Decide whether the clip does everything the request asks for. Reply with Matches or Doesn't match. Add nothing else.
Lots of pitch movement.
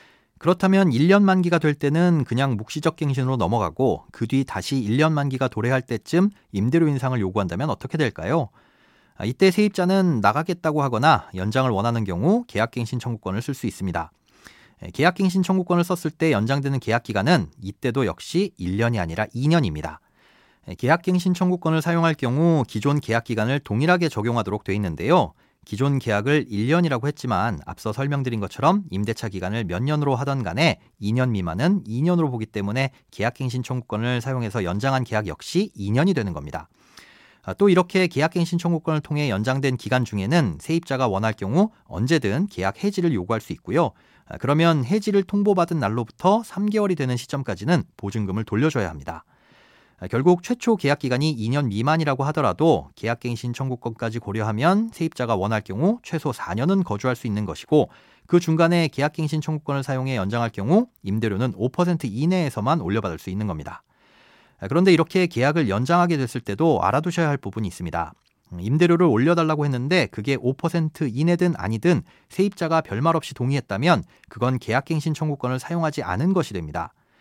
Matches